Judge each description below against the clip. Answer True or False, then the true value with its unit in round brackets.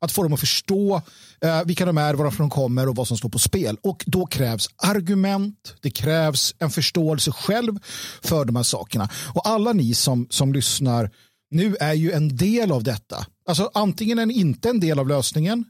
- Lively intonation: True (6.8 semitones)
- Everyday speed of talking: False (205 wpm)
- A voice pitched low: False (155 Hz)